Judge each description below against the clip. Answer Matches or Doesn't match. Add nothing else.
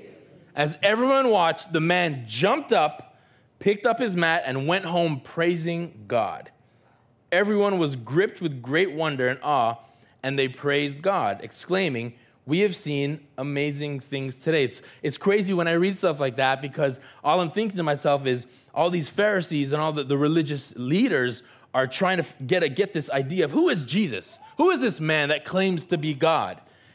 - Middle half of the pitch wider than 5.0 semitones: Matches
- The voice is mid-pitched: Matches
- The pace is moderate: Matches